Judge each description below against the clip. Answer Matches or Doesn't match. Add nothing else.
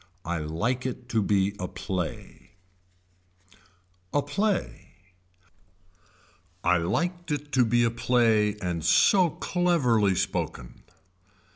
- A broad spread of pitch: Matches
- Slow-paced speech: Matches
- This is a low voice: Matches